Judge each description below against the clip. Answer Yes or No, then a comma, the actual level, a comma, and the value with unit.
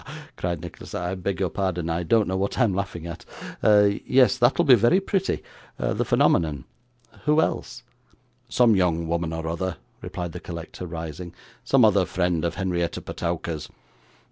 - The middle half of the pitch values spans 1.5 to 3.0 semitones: No, average, 3.5 semitones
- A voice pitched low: Yes, very low, 90 Hz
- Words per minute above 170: No, average, 155 wpm